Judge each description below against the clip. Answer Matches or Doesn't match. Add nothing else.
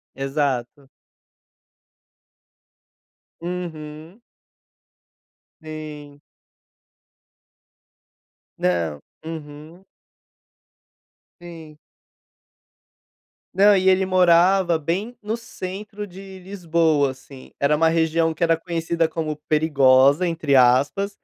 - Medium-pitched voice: Matches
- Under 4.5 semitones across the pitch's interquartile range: Matches